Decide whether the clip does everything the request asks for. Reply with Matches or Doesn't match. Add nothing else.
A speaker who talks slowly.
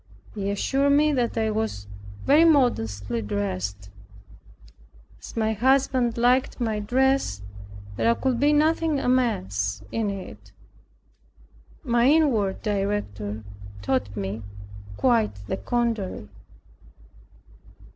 Matches